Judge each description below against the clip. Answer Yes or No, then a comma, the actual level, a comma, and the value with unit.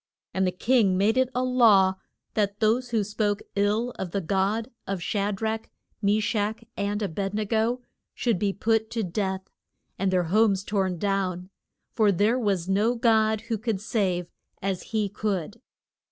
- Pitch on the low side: No, high, 205 Hz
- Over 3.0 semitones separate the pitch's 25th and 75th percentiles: No, narrow, 2.5 semitones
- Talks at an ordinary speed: Yes, average, 170 wpm